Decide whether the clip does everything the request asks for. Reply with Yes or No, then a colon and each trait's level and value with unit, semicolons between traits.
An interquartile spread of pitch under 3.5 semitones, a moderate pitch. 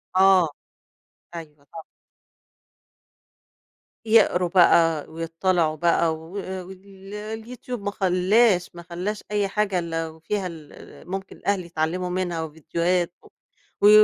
Yes: average, 3.1 semitones; medium, 180 Hz